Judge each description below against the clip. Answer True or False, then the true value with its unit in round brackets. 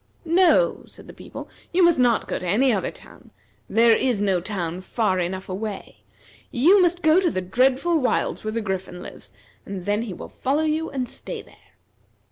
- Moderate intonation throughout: False (8.6 semitones)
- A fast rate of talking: False (190 wpm)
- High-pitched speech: True (230 Hz)